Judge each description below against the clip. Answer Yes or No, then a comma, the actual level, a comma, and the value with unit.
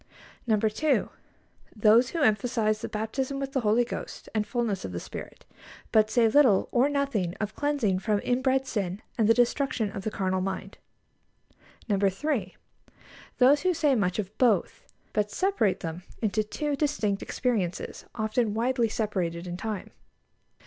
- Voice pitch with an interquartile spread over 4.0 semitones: Yes, average, 4.4 semitones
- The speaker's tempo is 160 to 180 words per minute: No, average, 150 wpm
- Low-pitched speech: No, high, 220 Hz